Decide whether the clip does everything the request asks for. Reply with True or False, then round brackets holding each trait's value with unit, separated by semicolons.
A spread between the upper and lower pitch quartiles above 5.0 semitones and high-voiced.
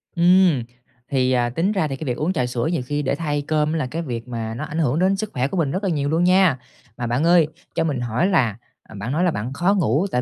False (5.6 semitones; 150 Hz)